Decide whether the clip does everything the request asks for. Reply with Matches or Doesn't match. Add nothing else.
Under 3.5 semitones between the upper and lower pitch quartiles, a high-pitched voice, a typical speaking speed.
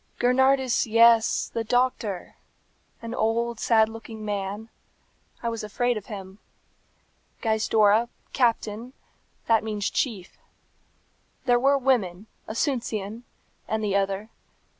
Doesn't match